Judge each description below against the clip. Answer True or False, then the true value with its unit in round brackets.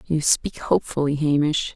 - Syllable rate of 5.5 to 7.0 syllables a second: False (4.9 syllables/s)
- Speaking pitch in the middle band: True (150 Hz)